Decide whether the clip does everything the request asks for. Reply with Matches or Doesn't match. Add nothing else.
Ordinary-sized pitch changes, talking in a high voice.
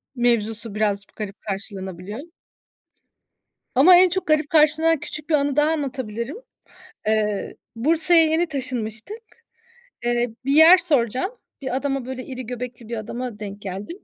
Doesn't match